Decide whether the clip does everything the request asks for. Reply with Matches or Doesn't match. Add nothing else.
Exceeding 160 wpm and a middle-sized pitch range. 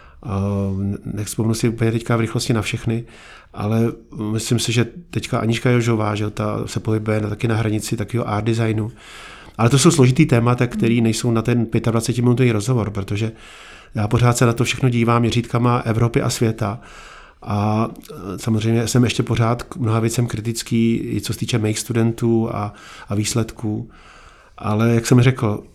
Doesn't match